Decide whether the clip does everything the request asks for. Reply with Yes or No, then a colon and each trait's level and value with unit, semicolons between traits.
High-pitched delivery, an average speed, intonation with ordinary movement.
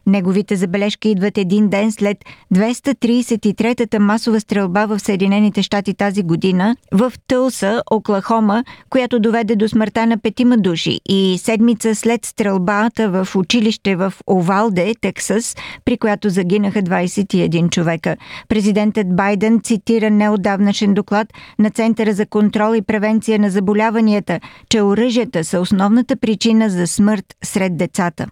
No: high, 210 Hz; average, 125 wpm; narrow, 2.1 semitones